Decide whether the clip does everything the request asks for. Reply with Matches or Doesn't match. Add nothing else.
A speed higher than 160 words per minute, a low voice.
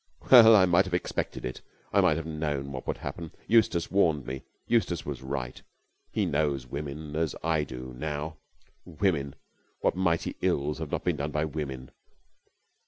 Matches